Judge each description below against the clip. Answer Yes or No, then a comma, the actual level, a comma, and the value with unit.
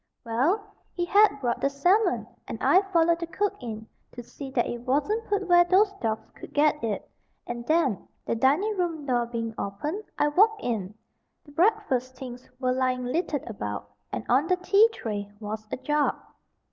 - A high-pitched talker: Yes, very high, 275 Hz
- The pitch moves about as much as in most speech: No, wide, 7.2 semitones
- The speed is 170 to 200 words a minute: Yes, average, 180 wpm